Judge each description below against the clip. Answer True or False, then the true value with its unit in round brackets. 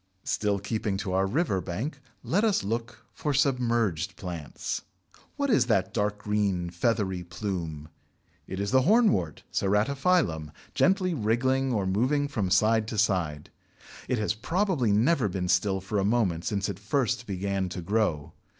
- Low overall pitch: True (105 Hz)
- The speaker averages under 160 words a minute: True (150 wpm)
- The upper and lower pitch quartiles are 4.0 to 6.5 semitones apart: True (5.1 semitones)